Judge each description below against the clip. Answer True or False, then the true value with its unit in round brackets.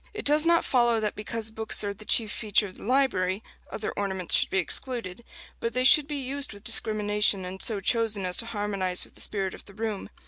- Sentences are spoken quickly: True (220 wpm)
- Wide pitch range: False (3.2 semitones)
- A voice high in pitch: True (215 Hz)